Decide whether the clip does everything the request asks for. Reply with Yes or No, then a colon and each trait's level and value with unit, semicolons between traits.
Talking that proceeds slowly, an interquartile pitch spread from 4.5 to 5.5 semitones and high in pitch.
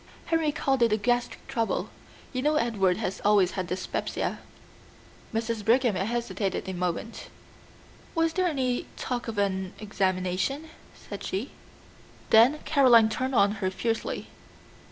Yes: slow, 130 wpm; average, 4.8 semitones; high, 225 Hz